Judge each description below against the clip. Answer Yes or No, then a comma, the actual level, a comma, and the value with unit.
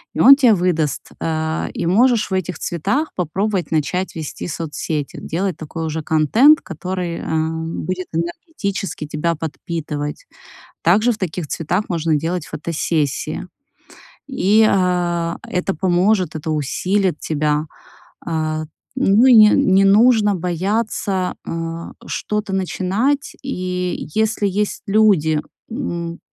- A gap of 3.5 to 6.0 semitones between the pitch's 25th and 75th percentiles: Yes, average, 4.2 semitones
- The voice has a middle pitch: Yes, medium, 180 Hz